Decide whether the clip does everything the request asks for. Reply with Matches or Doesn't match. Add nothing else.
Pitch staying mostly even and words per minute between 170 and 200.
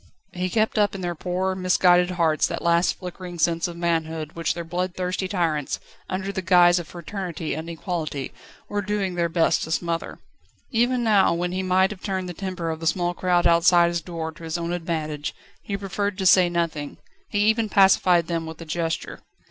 Matches